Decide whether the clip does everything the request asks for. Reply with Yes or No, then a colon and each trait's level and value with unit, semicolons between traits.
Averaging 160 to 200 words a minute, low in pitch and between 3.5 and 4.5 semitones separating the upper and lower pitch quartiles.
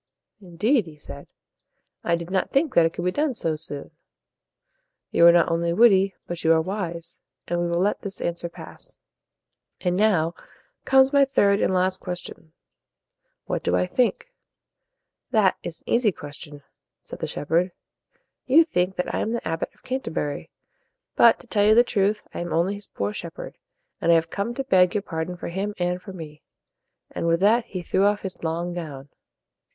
No: average, 195 wpm; medium, 180 Hz; average, 3.8 semitones